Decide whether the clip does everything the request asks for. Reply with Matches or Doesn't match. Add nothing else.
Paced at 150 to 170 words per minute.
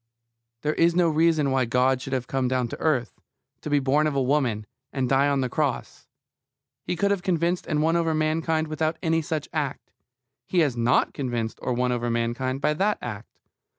Doesn't match